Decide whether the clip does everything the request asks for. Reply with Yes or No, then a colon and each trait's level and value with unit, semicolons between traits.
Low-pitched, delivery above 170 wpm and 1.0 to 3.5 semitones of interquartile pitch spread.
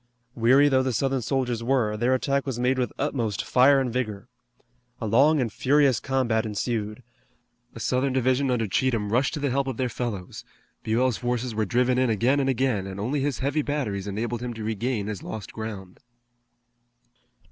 Yes: low, 125 Hz; average, 180 wpm; average, 3.2 semitones